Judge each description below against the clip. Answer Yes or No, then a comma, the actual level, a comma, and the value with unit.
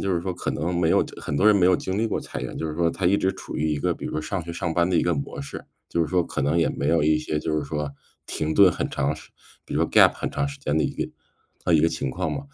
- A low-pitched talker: Yes, very low, 80 Hz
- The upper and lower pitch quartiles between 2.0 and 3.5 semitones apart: Yes, average, 3.1 semitones